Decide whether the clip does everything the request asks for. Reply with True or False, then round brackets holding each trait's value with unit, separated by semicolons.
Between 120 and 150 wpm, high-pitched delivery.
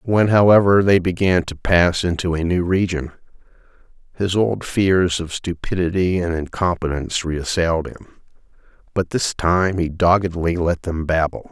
False (140 wpm; 90 Hz)